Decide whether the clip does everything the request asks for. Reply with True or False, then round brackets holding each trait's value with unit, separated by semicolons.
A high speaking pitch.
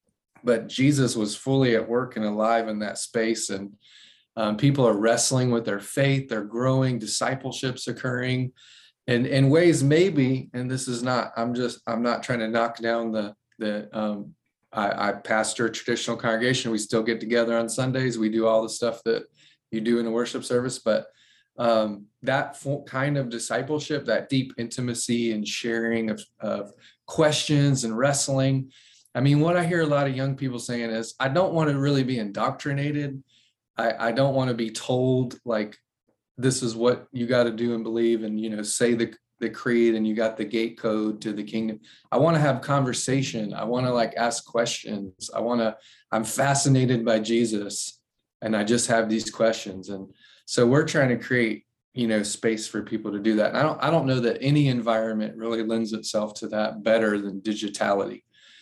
False (115 Hz)